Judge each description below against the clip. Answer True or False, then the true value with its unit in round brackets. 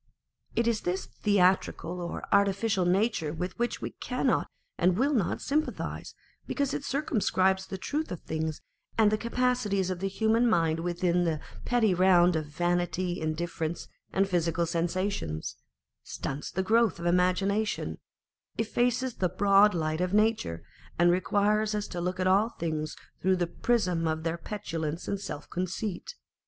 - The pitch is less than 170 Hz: False (185 Hz)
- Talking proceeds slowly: False (150 wpm)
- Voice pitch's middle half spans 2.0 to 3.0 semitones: False (3.8 semitones)